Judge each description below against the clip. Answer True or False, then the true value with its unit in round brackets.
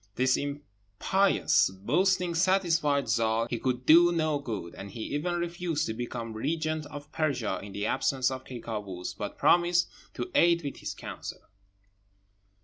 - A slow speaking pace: False (150 wpm)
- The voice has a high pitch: False (140 Hz)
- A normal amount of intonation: False (6.9 semitones)